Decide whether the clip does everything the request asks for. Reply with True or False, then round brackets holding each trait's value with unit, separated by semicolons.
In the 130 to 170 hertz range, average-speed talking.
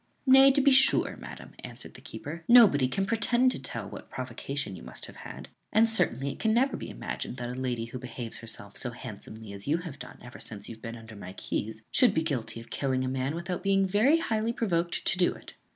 False (140 Hz; 230 wpm)